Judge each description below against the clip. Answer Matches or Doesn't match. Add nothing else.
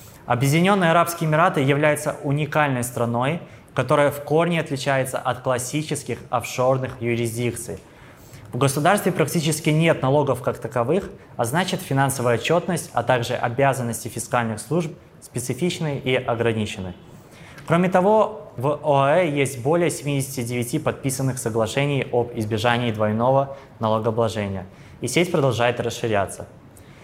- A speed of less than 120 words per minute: Matches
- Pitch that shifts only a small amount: Doesn't match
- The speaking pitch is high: Doesn't match